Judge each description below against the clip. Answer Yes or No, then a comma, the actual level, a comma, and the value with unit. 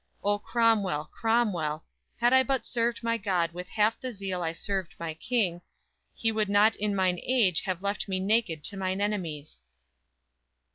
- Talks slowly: No, average, 170 wpm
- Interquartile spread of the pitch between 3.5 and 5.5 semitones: Yes, average, 4.1 semitones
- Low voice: No, high, 200 Hz